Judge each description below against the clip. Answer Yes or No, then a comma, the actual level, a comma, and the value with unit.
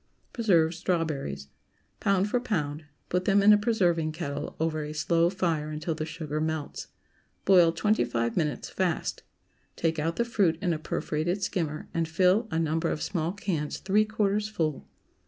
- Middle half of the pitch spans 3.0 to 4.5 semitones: Yes, average, 3.9 semitones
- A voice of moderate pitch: Yes, medium, 165 Hz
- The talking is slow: No, average, 170 wpm